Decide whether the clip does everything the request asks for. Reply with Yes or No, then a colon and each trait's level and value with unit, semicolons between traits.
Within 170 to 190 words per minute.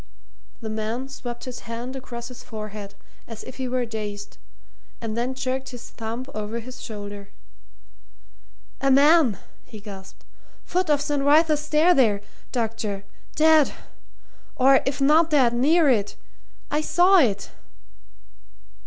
No: slow, 135 wpm